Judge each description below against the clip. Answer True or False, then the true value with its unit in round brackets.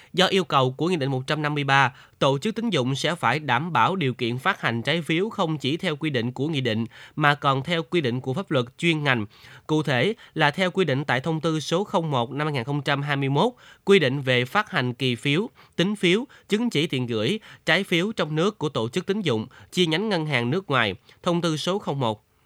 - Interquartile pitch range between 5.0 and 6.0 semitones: True (5.6 semitones)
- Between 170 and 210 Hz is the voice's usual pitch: False (150 Hz)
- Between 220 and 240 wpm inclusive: True (225 wpm)